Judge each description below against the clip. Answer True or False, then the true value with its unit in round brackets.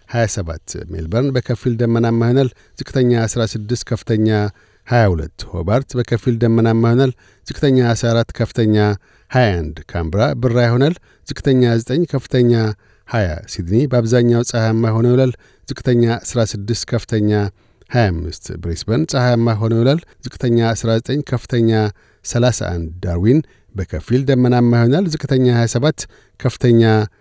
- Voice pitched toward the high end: False (115 Hz)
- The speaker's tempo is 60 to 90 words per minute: False (105 wpm)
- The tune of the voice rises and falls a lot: False (2.8 semitones)